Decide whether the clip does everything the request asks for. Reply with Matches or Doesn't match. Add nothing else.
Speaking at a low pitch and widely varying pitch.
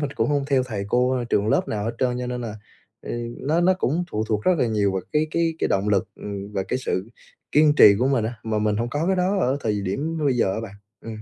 Matches